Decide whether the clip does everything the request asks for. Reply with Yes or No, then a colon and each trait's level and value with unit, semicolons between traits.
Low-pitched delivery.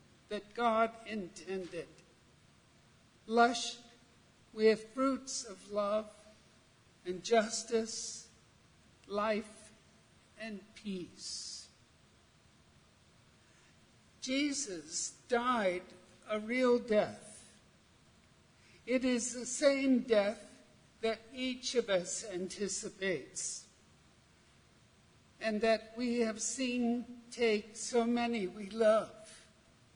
No: high, 225 Hz